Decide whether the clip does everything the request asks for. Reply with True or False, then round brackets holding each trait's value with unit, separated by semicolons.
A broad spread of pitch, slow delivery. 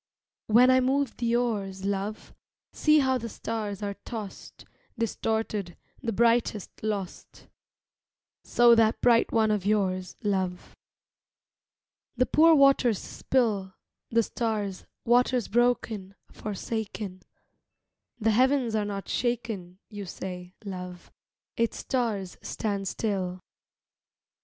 False (3.5 semitones; 110 wpm)